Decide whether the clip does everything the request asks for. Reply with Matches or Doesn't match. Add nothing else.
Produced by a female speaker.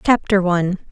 Matches